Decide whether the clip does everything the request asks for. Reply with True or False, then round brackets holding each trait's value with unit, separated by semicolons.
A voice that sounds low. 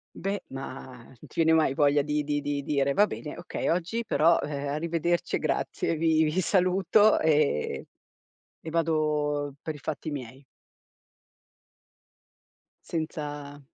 False (150 Hz)